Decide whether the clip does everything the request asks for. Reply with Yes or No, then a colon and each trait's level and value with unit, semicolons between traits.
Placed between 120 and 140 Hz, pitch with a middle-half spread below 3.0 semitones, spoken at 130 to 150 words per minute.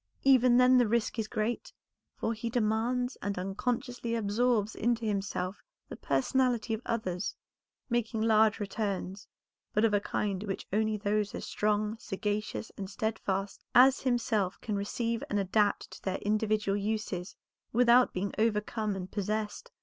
No: high, 215 Hz; narrow, 2.5 semitones; average, 145 wpm